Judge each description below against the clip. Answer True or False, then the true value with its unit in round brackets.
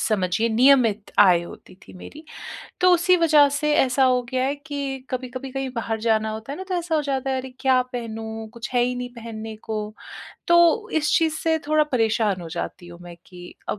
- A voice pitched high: True (250 Hz)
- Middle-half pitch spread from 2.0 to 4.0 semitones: False (4.7 semitones)